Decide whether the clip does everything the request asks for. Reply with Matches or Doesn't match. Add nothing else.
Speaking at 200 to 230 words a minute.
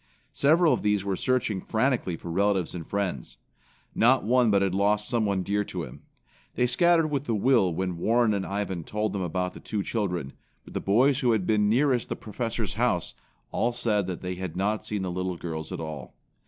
Matches